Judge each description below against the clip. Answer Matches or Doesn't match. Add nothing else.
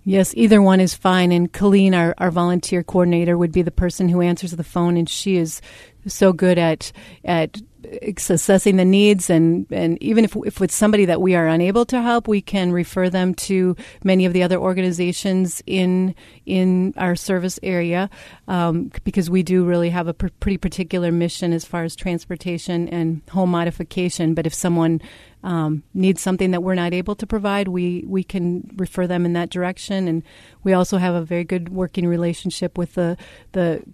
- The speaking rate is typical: Matches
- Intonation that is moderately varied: Doesn't match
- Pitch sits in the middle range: Matches